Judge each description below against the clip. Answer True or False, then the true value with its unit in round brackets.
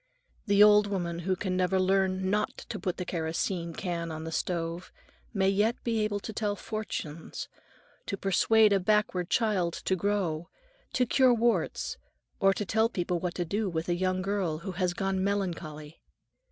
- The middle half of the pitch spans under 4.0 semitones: True (3.1 semitones)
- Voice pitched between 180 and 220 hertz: True (190 Hz)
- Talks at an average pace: True (175 wpm)